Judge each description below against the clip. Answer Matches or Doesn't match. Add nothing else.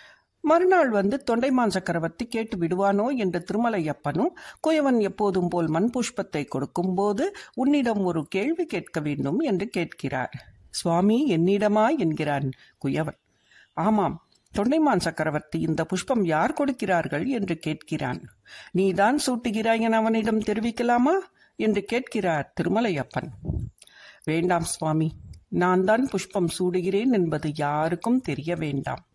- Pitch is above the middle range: Matches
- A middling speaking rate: Doesn't match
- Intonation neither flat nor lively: Doesn't match